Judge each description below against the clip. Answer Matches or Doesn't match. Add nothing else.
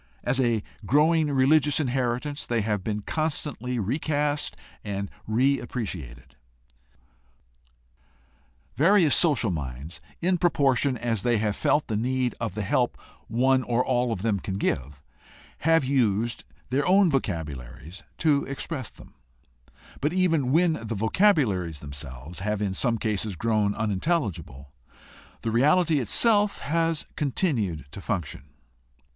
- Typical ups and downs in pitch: Doesn't match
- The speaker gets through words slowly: Matches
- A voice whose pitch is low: Matches